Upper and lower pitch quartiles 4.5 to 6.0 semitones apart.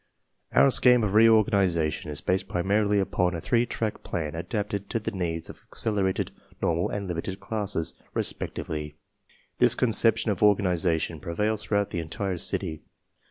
No: average, 3.9 semitones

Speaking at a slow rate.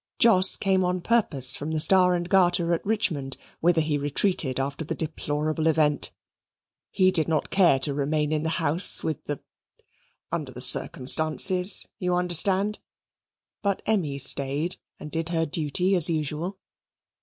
No: average, 150 wpm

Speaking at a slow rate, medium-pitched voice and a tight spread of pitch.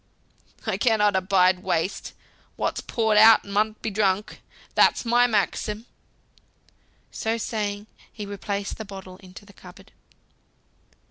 No: slow, 120 wpm; high, 205 Hz; narrow, 2.2 semitones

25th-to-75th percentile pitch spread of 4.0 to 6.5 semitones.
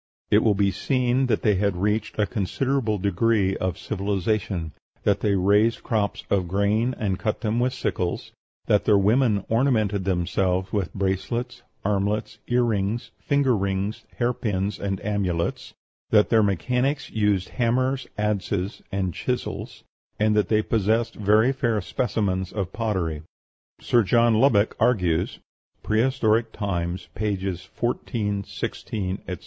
No: average, 3.1 semitones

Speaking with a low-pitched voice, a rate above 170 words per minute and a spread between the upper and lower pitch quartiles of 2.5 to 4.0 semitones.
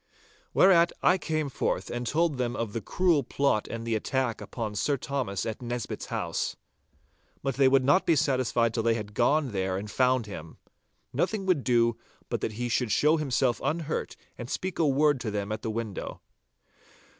No: low, 125 Hz; average, 185 wpm; average, 4.4 semitones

